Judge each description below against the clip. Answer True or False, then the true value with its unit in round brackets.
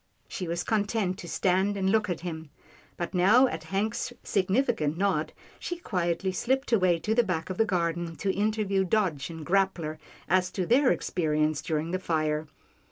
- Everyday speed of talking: True (170 wpm)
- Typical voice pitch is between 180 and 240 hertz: True (185 Hz)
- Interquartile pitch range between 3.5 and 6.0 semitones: True (3.8 semitones)